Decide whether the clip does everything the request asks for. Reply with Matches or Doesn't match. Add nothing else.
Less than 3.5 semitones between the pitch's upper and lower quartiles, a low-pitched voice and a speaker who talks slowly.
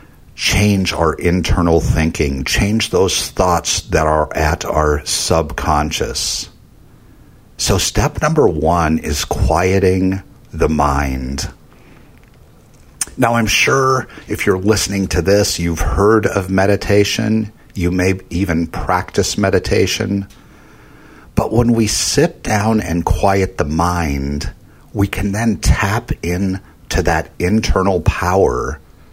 Doesn't match